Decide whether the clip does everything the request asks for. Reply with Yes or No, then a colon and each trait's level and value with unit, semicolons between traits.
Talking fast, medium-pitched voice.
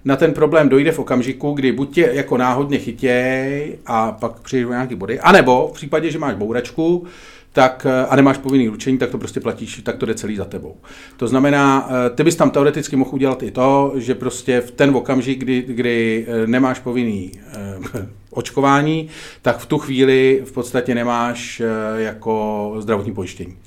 No: fast, 175 wpm; low, 130 Hz